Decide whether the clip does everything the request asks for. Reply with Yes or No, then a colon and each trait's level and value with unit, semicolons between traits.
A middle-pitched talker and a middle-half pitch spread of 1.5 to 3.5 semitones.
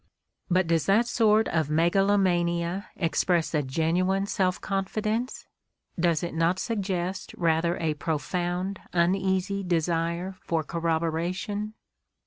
Yes: medium, 175 Hz; average, 2.8 semitones